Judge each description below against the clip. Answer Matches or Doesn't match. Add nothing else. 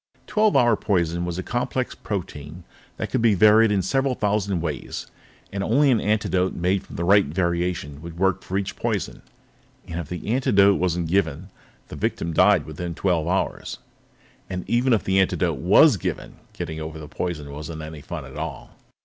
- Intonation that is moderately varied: Matches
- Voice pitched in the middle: Doesn't match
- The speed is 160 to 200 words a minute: Matches